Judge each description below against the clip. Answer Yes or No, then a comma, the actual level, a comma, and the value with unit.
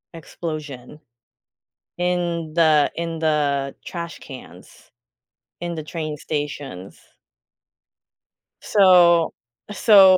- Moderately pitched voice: Yes, medium, 160 Hz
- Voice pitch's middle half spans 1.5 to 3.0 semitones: Yes, average, 2.7 semitones